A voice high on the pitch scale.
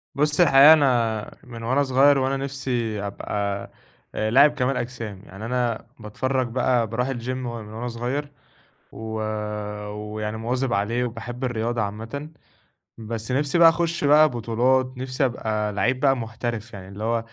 No: low, 120 Hz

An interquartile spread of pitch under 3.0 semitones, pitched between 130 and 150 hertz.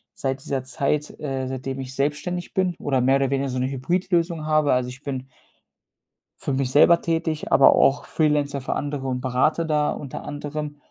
Yes: narrow, 2.5 semitones; medium, 140 Hz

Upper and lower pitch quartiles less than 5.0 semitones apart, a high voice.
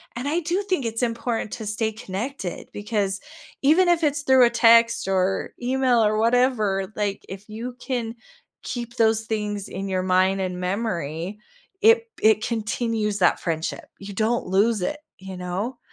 Yes: average, 3.9 semitones; high, 220 Hz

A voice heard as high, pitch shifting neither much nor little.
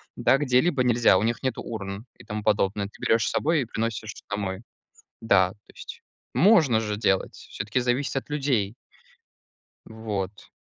No: low, 110 Hz; average, 4.0 semitones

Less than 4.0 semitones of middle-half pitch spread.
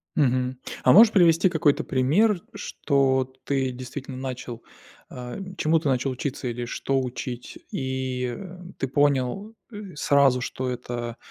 Yes: narrow, 2.5 semitones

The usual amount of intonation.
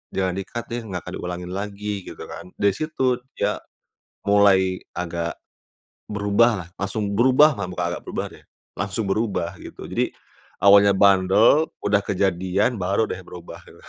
No: narrow, 2.1 semitones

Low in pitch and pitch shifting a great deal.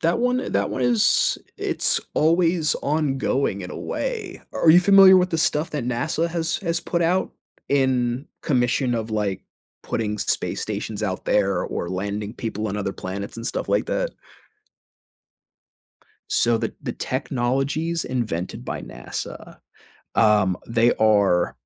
Yes: low, 125 Hz; wide, 7.7 semitones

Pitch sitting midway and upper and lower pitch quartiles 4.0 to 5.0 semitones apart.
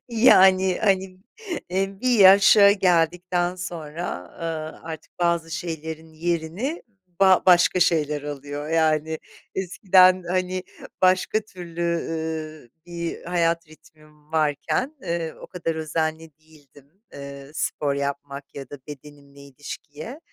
No: medium, 165 Hz; average, 3.4 semitones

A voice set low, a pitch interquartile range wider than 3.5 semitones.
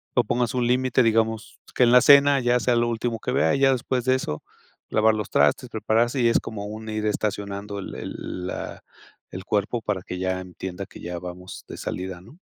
Yes: low, 110 Hz; average, 3.9 semitones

